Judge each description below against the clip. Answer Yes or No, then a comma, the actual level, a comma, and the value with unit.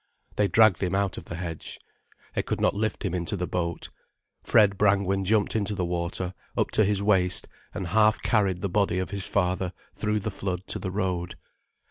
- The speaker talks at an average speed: Yes, average, 195 wpm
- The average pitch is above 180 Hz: No, very low, 95 Hz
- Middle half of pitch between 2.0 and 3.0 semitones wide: Yes, narrow, 2.4 semitones